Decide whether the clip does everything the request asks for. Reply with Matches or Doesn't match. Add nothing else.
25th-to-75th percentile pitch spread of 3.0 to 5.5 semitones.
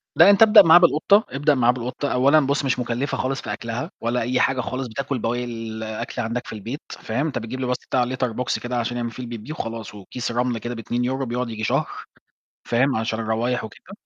Doesn't match